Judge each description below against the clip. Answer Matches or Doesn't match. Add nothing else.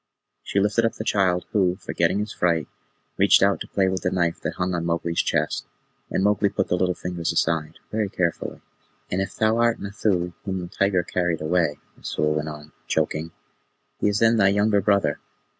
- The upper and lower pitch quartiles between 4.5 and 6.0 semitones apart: Doesn't match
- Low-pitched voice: Matches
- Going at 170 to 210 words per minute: Matches